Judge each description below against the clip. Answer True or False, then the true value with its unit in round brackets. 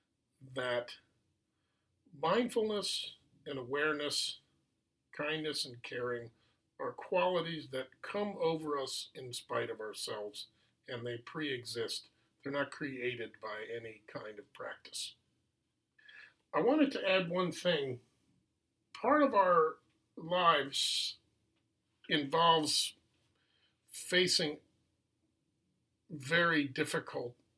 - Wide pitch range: True (6.6 semitones)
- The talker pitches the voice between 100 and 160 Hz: True (140 Hz)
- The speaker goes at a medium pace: False (95 wpm)